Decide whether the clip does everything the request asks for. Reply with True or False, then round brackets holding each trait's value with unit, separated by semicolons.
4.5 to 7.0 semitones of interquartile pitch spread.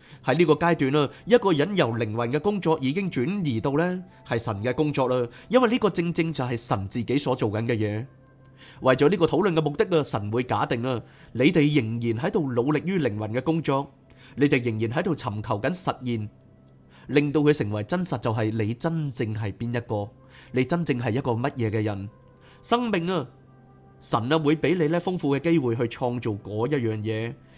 True (5.2 semitones)